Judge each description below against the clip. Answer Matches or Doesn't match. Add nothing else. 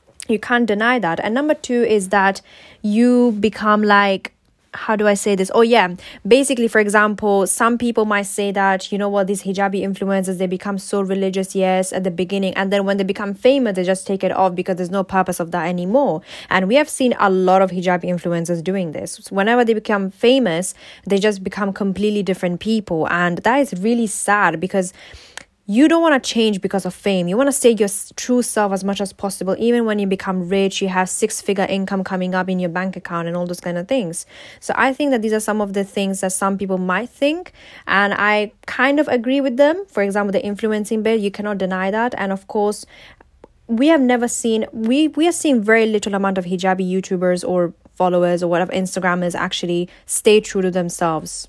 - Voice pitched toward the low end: Doesn't match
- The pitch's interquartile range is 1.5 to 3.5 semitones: Matches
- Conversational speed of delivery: Doesn't match